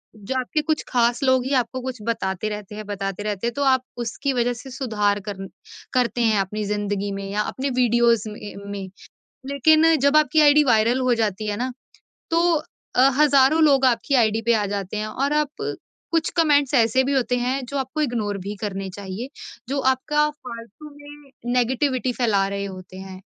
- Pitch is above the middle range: Yes, high, 240 Hz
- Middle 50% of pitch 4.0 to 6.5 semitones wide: Yes, average, 4.9 semitones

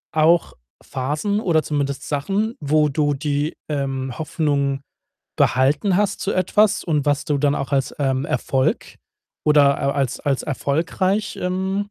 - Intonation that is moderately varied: Yes, average, 4.5 semitones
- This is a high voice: No, medium, 150 Hz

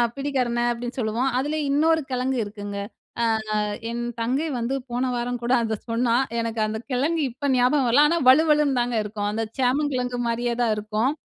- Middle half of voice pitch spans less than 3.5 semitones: Yes, average, 3.1 semitones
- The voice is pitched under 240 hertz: No, high, 245 Hz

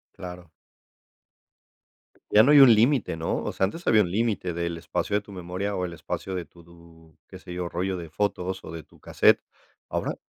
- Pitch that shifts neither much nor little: Yes, average, 3.2 semitones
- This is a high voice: No, very low, 90 Hz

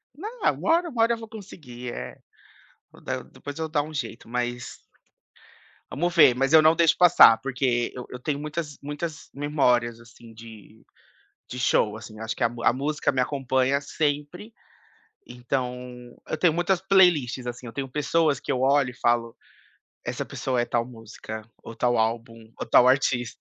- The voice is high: No, low, 130 Hz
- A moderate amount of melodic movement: Yes, average, 4.2 semitones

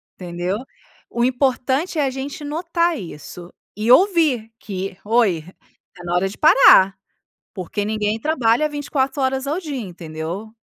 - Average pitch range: No, wide, 7.2 semitones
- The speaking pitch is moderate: No, high, 235 Hz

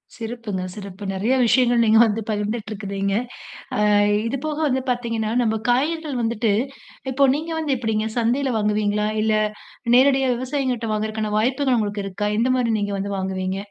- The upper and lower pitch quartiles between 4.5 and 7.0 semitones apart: No, average, 3.5 semitones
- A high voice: Yes, high, 225 Hz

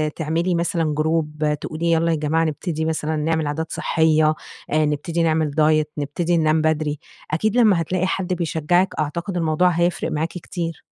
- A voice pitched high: No, medium, 160 Hz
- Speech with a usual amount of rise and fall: No, narrow, 1.8 semitones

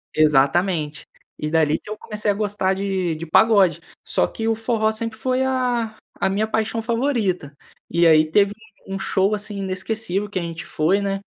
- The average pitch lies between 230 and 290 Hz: No, high, 200 Hz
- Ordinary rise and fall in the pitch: Yes, average, 4.2 semitones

